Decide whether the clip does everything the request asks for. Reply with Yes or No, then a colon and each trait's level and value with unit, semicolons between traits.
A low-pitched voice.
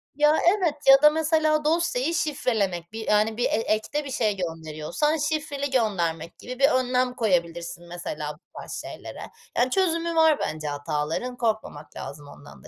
No: high, 245 Hz